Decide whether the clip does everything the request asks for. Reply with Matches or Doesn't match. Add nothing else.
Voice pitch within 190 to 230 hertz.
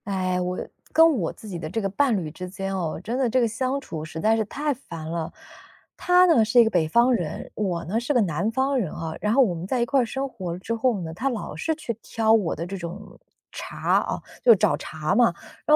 Matches